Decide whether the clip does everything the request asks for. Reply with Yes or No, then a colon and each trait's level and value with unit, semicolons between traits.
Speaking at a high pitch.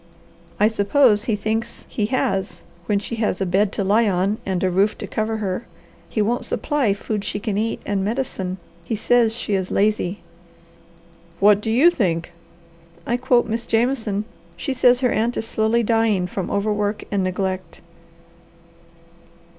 Yes: high, 210 Hz